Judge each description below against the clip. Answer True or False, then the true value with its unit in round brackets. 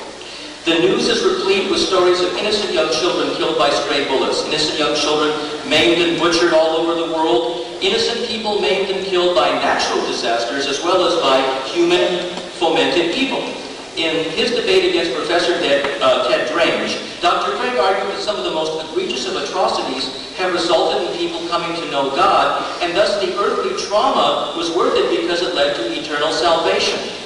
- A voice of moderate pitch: True (175 Hz)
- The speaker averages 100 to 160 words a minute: False (175 wpm)